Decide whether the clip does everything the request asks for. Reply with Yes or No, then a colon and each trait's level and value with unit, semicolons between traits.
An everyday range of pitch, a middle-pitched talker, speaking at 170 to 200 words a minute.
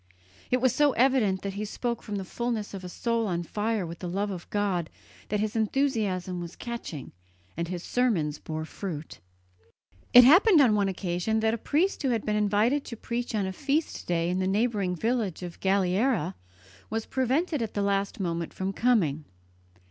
No: average, 4.7 semitones; high, 205 Hz; average, 185 wpm